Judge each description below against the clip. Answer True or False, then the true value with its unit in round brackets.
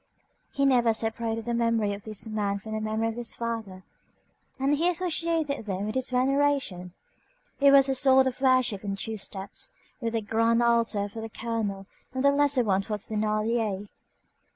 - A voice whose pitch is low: False (230 Hz)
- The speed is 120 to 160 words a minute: False (175 wpm)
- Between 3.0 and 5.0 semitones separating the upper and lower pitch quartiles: True (3.7 semitones)